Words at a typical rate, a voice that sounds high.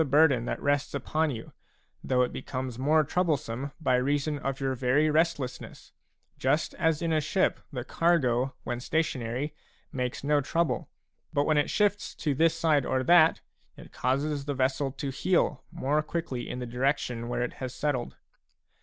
No: average, 170 wpm; medium, 140 Hz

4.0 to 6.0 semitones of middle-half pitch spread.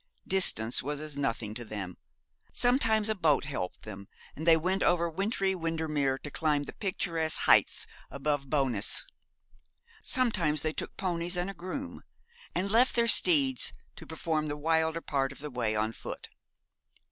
Yes: average, 4.9 semitones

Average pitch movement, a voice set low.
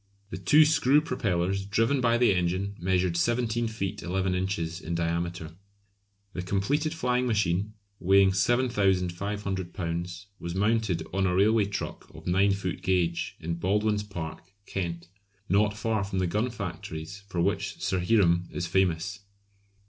Yes: average, 3.4 semitones; very low, 95 Hz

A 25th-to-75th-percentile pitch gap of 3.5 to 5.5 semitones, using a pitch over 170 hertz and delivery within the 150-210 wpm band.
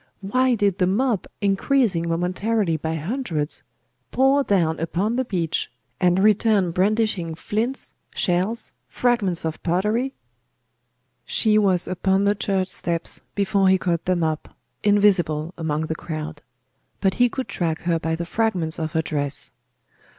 No: average, 4.4 semitones; medium, 185 Hz; average, 140 wpm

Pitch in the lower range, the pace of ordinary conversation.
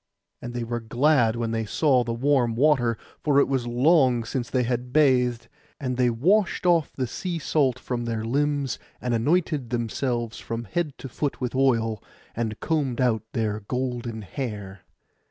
Yes: low, 125 Hz; average, 170 wpm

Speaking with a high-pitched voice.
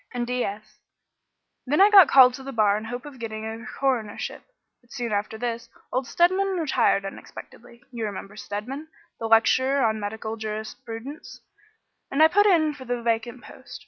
Yes: high, 240 Hz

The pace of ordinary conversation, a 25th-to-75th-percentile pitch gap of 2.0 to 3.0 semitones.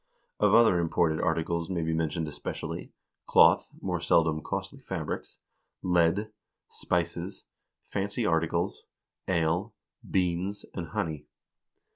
No: slow, 105 wpm; narrow, 2.5 semitones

